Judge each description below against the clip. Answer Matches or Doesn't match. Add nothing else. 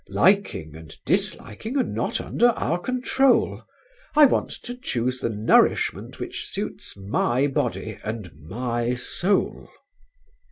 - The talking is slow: Matches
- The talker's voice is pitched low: Matches